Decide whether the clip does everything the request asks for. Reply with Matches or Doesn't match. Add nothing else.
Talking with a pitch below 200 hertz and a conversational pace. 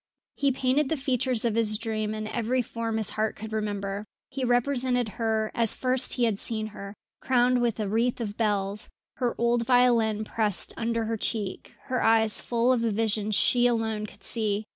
Doesn't match